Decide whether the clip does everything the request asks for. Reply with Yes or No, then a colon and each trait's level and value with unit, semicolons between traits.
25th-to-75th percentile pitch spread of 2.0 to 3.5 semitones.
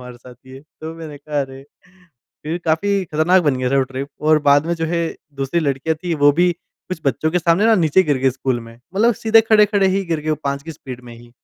No: average, 4.4 semitones